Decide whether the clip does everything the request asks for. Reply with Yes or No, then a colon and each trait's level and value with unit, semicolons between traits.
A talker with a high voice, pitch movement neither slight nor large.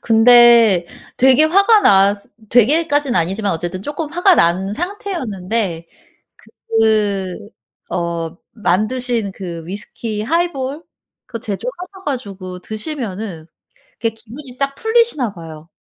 No: high, 225 Hz; wide, 7.1 semitones